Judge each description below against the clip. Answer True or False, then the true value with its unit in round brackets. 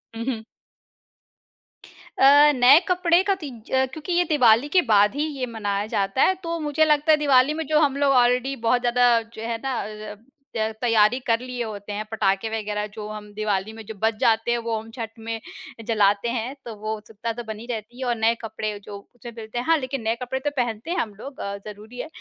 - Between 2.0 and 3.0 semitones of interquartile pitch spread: False (3.6 semitones)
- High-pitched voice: True (230 Hz)